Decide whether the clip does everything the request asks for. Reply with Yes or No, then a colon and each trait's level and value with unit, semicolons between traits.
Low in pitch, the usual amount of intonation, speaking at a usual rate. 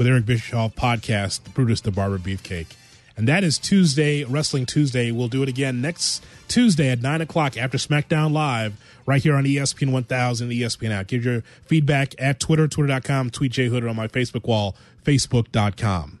Yes: low, 130 Hz; average, 3.7 semitones; average, 175 wpm